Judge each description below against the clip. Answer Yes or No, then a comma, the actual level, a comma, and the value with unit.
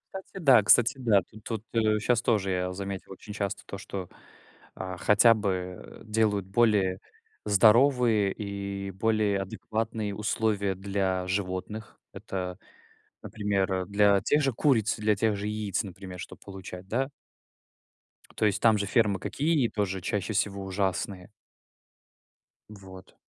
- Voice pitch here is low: Yes, low, 100 Hz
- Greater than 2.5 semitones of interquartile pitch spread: No, narrow, 2.2 semitones